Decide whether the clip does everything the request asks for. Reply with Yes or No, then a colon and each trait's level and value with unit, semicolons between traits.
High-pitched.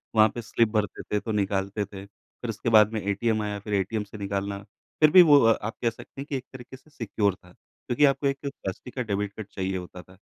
No: low, 105 Hz